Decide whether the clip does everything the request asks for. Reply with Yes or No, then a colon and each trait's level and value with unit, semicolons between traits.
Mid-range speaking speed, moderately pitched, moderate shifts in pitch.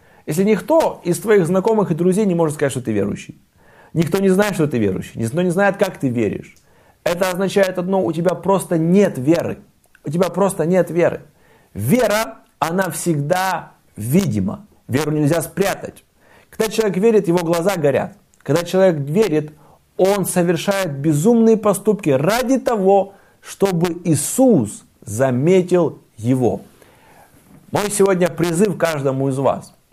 Yes: average, 140 wpm; medium, 180 Hz; average, 4.4 semitones